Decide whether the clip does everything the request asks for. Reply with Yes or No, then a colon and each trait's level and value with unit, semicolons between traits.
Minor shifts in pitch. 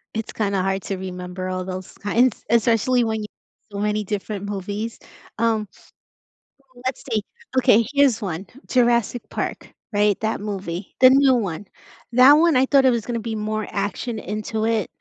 No: average, 3.1 semitones